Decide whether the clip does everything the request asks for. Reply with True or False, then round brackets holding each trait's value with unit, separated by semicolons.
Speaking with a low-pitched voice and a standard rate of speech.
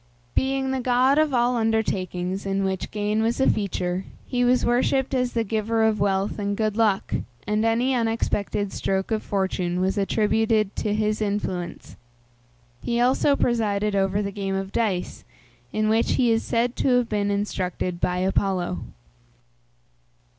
False (215 Hz; 155 wpm)